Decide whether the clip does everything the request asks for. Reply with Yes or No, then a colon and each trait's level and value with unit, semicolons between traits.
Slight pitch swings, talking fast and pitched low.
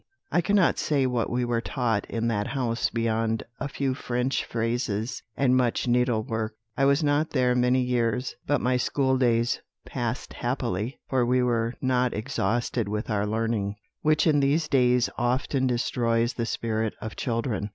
No: narrow, 2.3 semitones; average, 160 wpm; low, 125 Hz